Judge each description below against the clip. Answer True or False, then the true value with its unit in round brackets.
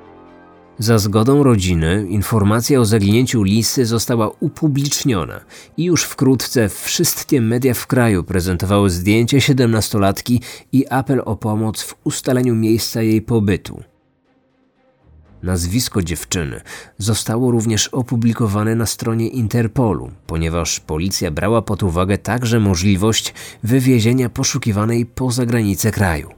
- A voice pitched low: True (110 Hz)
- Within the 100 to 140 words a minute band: True (110 wpm)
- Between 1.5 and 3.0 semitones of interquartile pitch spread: False (3.6 semitones)